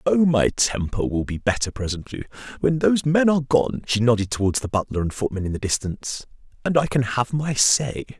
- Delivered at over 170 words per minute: Yes, average, 190 wpm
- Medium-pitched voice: No, low, 125 Hz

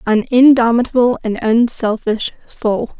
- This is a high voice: Yes, high, 230 Hz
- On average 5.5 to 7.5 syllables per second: No, 4.2 syllables/s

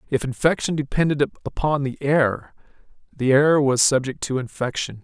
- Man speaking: Yes, male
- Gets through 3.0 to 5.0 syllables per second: Yes, 4.7 syllables/s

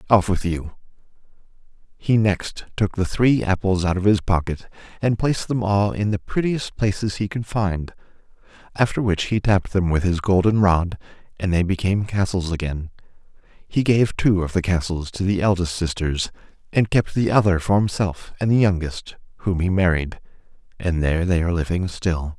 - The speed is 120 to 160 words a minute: No, average, 175 wpm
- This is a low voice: Yes, very low, 95 Hz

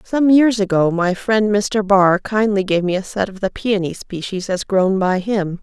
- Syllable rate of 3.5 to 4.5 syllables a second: Yes, 4.3 syllables/s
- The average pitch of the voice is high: Yes, high, 200 Hz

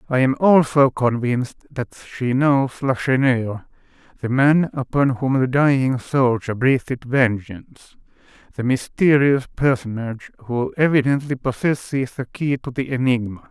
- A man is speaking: Yes, male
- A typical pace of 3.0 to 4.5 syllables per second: Yes, 4.3 syllables/s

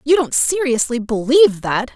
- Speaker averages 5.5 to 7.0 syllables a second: No, 4.9 syllables/s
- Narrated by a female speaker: Yes, female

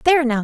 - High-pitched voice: Yes, very high, 275 Hz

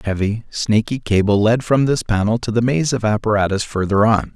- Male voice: Yes, male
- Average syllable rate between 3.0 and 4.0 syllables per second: No, 5.4 syllables/s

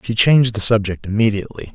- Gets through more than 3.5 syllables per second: Yes, 6.7 syllables/s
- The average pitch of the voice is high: No, low, 110 Hz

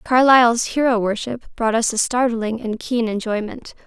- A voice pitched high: Yes, high, 230 Hz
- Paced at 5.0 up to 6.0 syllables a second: No, 4.7 syllables/s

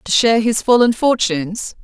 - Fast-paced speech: No, average, 165 wpm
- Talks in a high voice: Yes, high, 220 Hz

